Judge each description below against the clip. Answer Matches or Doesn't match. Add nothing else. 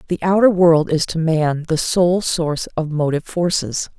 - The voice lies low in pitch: Doesn't match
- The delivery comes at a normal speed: Matches